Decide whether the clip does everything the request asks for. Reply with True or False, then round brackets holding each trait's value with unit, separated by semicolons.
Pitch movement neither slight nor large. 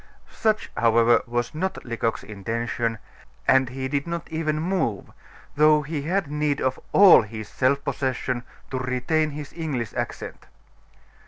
True (4.6 semitones)